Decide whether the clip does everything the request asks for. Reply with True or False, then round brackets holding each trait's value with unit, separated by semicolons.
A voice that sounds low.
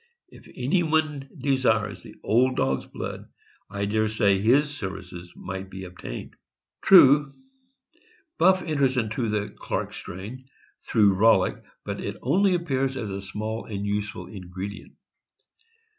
True (110 Hz)